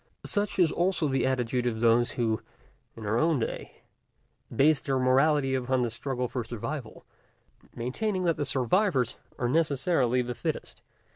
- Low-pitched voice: Yes, low, 130 Hz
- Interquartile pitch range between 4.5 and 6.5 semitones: No, average, 4.1 semitones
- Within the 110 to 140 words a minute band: No, average, 150 wpm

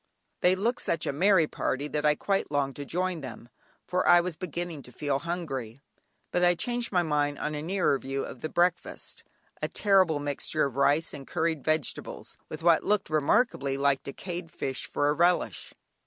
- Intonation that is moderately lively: Yes, average, 3.9 semitones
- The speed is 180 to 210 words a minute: Yes, average, 185 wpm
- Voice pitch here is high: No, medium, 155 Hz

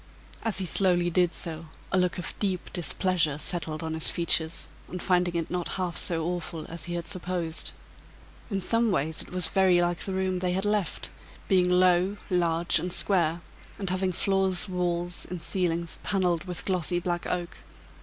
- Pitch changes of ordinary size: No, narrow, 1.5 semitones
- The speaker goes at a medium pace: Yes, average, 175 wpm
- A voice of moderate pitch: Yes, medium, 180 Hz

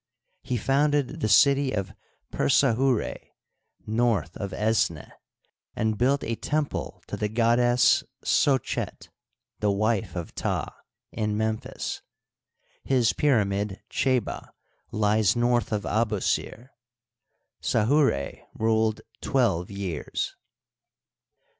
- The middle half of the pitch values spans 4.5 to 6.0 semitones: No, average, 3.3 semitones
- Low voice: Yes, low, 110 Hz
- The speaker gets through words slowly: Yes, slow, 95 wpm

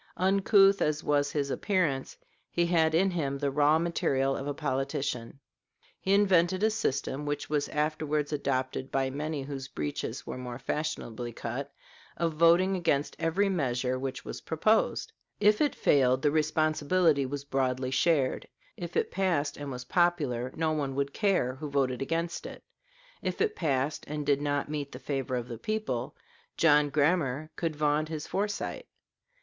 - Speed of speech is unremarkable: Yes, average, 160 wpm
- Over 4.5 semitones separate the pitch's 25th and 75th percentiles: No, average, 3.7 semitones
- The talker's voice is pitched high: No, medium, 145 Hz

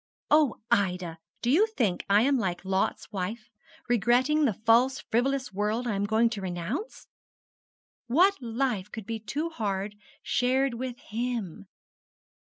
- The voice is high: Yes, high, 230 Hz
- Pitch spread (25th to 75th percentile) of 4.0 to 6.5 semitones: Yes, average, 4.5 semitones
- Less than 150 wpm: Yes, average, 140 wpm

